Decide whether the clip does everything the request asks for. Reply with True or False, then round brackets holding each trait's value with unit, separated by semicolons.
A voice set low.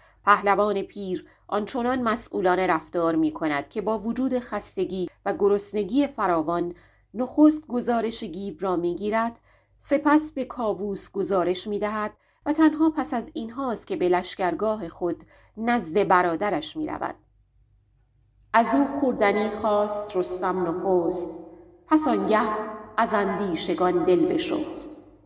False (210 Hz)